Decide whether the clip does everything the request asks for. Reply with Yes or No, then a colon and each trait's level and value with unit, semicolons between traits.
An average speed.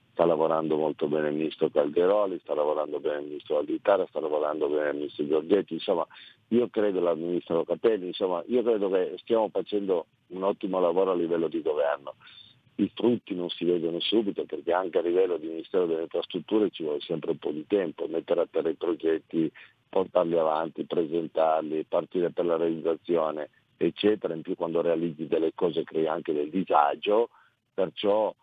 No: fast, 175 wpm